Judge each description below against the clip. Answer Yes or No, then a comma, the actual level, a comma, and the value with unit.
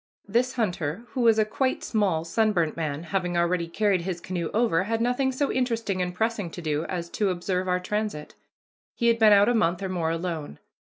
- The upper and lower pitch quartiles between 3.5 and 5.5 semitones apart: Yes, average, 4.7 semitones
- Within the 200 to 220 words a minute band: Yes, fast, 205 wpm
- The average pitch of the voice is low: No, medium, 185 Hz